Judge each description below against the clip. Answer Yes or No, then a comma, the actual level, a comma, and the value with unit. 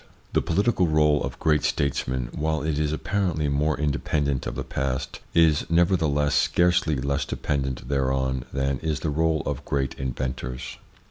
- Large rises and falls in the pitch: No, average, 2.7 semitones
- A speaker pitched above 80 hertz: No, very low, 75 Hz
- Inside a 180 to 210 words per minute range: No, average, 155 wpm